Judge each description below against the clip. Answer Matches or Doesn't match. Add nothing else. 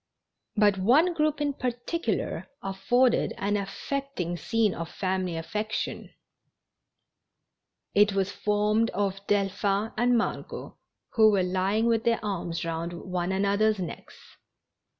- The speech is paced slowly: Matches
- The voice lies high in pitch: Matches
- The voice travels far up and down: Doesn't match